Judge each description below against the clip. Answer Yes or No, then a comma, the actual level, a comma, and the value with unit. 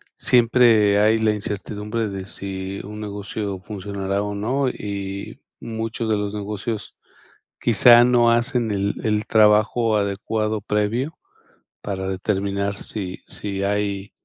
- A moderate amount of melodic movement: No, narrow, 2.0 semitones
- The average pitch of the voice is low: Yes, low, 105 Hz